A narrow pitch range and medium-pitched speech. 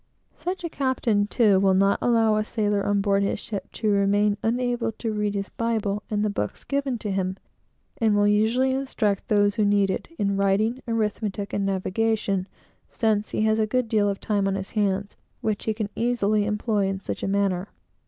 No: narrow, 2.1 semitones; high, 210 Hz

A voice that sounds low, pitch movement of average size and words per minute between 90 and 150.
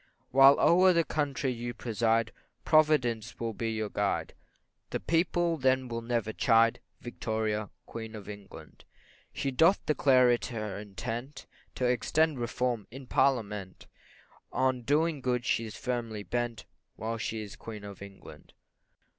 Yes: low, 120 Hz; average, 3.3 semitones; average, 140 wpm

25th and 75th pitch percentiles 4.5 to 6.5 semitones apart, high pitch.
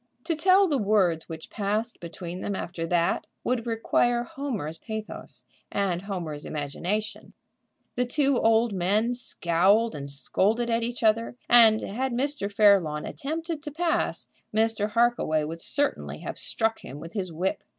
Yes: wide, 5.6 semitones; high, 215 Hz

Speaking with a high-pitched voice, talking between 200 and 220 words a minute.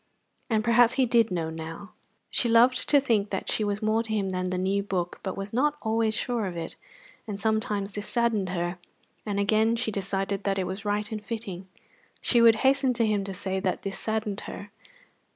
Yes: high, 210 Hz; fast, 205 wpm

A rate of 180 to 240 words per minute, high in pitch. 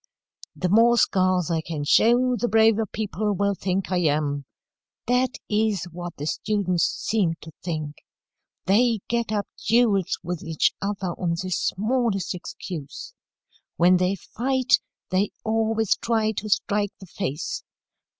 No: average, 140 wpm; high, 200 Hz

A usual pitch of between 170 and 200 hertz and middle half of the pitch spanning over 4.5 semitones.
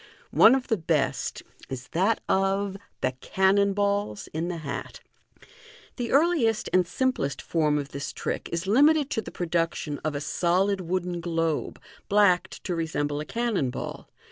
Yes: medium, 185 Hz; average, 4.9 semitones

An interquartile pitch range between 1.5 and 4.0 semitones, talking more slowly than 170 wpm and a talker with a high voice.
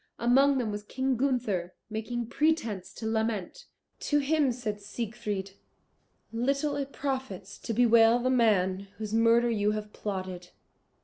Yes: average, 3.7 semitones; slow, 135 wpm; high, 230 Hz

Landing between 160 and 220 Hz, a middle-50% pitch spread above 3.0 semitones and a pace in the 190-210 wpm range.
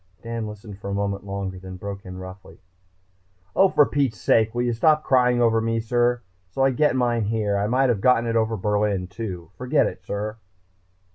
No: low, 110 Hz; average, 3.4 semitones; average, 195 wpm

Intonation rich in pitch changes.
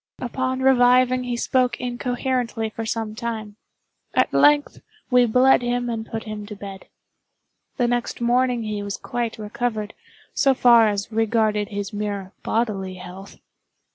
No: average, 2.8 semitones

